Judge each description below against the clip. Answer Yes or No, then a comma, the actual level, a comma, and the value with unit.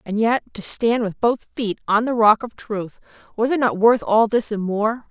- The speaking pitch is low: No, high, 220 Hz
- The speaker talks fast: Yes, fast, 225 wpm